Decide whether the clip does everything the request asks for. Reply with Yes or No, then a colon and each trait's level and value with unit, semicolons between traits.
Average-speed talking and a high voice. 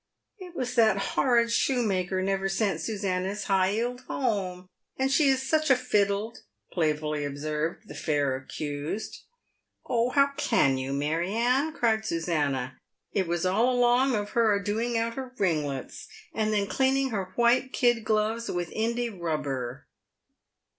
Yes: average, 150 wpm; high, 205 Hz